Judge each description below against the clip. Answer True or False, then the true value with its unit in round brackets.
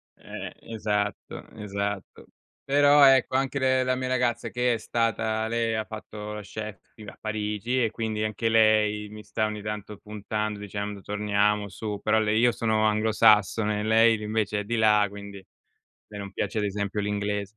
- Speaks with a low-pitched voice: True (105 Hz)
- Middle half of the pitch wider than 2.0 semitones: False (1.5 semitones)